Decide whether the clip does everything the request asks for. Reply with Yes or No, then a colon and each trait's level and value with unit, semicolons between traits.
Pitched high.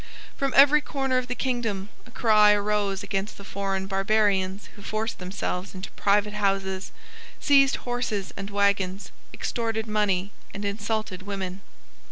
Yes: high, 205 Hz